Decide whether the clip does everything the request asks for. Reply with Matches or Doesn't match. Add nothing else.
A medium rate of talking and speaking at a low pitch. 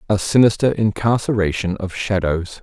Doesn't match